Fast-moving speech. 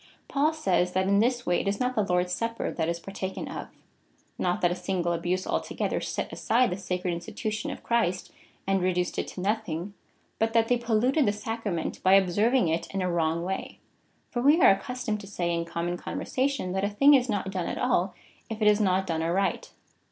Yes: fast, 210 wpm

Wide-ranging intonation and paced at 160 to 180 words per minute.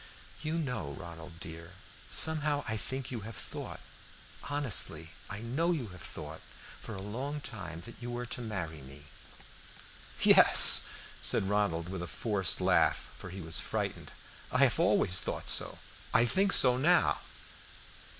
No: wide, 7.3 semitones; average, 150 wpm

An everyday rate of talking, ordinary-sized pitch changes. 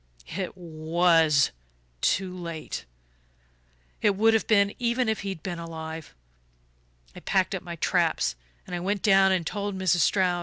Yes: average, 145 wpm; average, 3.3 semitones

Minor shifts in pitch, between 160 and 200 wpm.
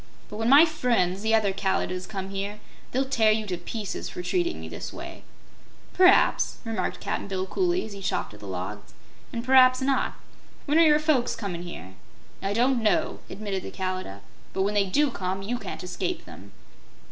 No: wide, 5.5 semitones; average, 190 wpm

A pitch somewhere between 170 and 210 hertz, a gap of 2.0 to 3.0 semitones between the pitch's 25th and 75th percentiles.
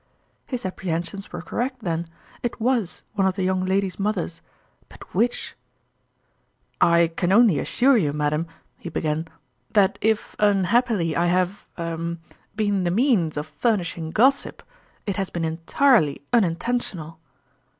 No: medium, 185 Hz; average, 4.7 semitones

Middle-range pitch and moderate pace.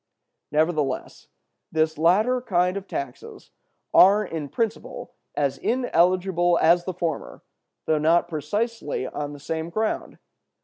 No: medium, 170 Hz; slow, 120 wpm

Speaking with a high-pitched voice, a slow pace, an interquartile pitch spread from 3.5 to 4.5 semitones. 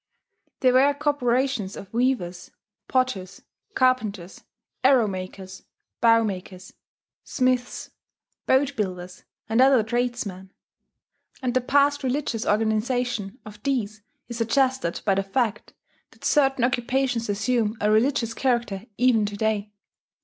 Yes: high, 235 Hz; slow, 115 wpm; average, 3.8 semitones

